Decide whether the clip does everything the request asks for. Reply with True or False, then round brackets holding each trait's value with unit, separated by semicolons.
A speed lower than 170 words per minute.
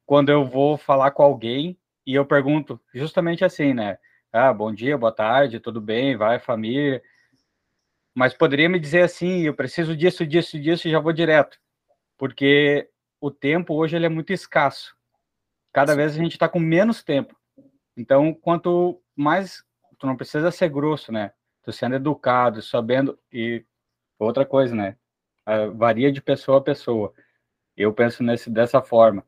True (160 wpm)